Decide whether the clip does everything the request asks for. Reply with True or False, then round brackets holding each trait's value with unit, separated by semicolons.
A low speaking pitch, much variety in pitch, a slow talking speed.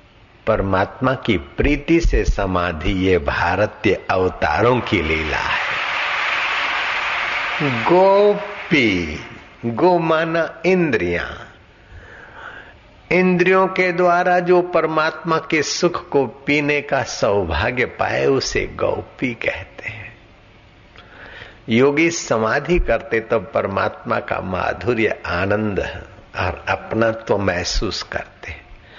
True (130 Hz; 8.0 semitones; 90 wpm)